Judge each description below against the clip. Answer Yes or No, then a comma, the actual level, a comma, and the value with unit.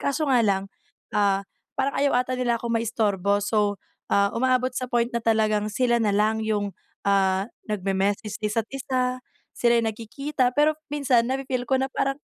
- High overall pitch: Yes, high, 230 Hz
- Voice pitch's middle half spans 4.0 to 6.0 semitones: No, average, 3.6 semitones